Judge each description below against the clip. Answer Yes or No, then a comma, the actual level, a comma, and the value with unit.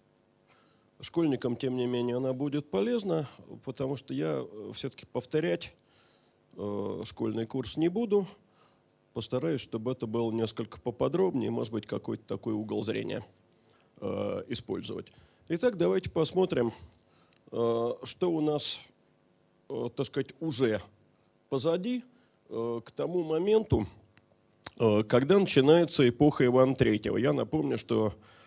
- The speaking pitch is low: Yes, low, 125 Hz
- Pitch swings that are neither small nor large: No, wide, 5.8 semitones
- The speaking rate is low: Yes, slow, 105 wpm